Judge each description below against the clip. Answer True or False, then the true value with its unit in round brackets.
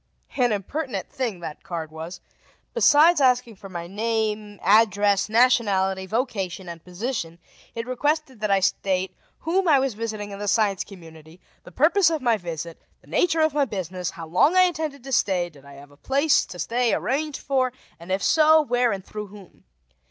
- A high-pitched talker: True (215 Hz)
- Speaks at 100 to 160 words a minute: False (180 wpm)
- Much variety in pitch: True (6.4 semitones)